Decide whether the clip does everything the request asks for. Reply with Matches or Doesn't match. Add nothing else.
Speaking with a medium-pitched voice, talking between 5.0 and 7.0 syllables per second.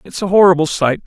Matches